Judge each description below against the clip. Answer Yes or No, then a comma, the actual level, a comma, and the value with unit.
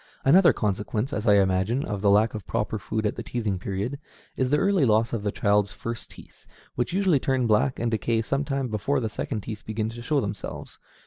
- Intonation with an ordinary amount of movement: Yes, average, 4.1 semitones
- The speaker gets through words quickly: Yes, fast, 215 wpm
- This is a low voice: Yes, low, 110 Hz